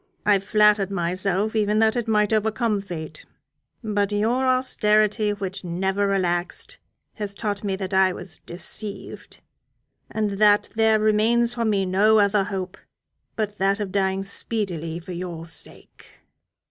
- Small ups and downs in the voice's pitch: Yes, narrow, 2.1 semitones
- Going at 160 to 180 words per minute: No, average, 140 wpm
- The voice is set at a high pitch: Yes, high, 205 Hz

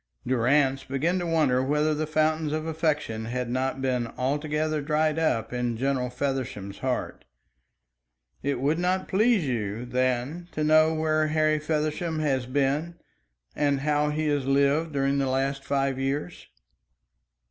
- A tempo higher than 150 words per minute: No, average, 145 wpm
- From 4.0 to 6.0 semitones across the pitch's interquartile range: No, average, 3.1 semitones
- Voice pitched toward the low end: No, medium, 145 Hz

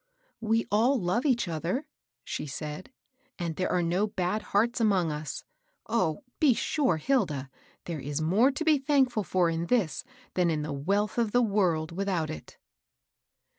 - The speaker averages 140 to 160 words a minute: No, average, 170 wpm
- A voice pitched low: No, medium, 185 Hz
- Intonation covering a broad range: Yes, wide, 6.4 semitones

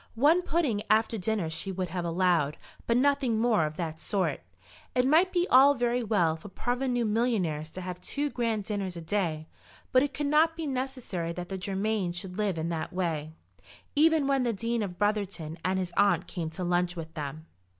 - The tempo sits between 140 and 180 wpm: No, average, 195 wpm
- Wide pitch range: Yes, wide, 6.1 semitones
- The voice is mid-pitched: No, high, 205 Hz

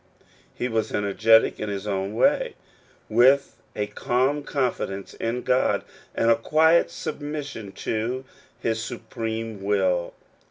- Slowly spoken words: Yes, slow, 125 wpm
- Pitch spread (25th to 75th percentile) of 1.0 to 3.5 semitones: No, average, 4.0 semitones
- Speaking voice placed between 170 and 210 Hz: No, low, 115 Hz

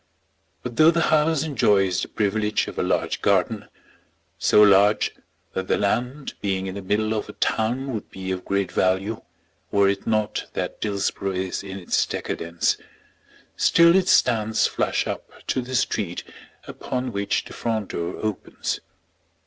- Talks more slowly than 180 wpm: Yes, average, 155 wpm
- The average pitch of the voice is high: No, low, 105 Hz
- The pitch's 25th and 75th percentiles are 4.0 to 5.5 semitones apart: No, average, 3.6 semitones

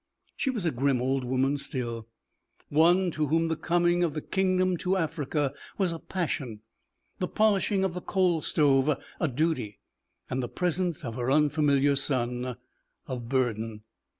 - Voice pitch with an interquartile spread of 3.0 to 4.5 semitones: No, average, 5.2 semitones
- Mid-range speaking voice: Yes, medium, 150 Hz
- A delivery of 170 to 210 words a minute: No, average, 155 wpm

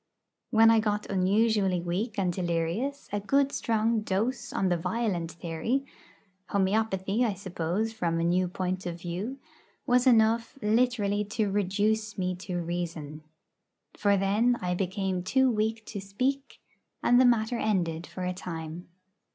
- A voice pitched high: Yes, high, 200 Hz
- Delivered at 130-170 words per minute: Yes, average, 145 wpm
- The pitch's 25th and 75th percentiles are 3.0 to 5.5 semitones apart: Yes, average, 3.8 semitones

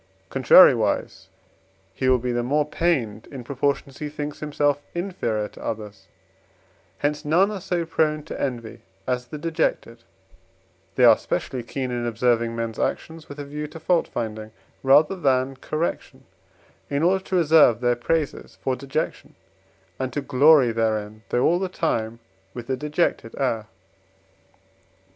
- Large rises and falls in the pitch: No, average, 4.4 semitones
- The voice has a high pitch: No, low, 135 Hz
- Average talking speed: Yes, average, 150 wpm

